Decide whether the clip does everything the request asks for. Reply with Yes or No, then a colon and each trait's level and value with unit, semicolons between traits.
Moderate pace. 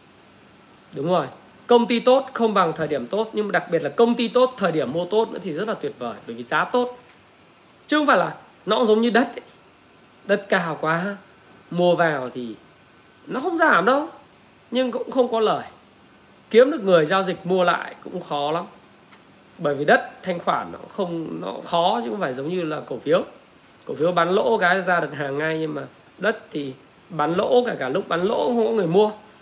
Yes: average, 220 wpm